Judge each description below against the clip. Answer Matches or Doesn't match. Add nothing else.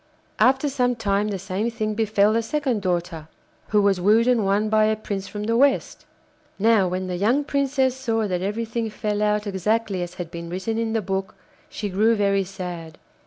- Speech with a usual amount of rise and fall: Matches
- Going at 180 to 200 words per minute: Matches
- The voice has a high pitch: Matches